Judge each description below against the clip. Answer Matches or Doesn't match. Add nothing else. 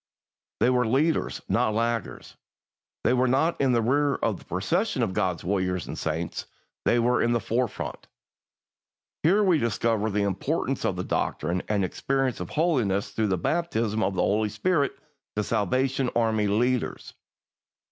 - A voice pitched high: Doesn't match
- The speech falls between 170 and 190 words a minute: Doesn't match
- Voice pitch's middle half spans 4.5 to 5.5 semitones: Matches